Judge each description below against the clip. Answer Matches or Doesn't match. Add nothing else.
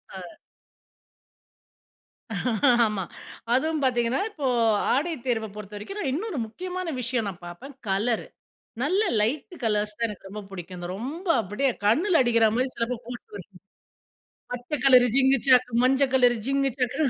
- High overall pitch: Matches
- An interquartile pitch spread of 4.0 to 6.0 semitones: Matches